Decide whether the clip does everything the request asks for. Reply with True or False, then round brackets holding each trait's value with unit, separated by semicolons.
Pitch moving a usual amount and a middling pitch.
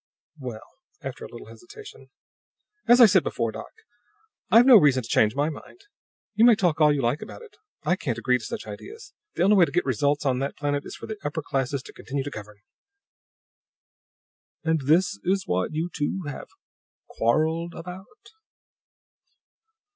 False (6.7 semitones; 150 Hz)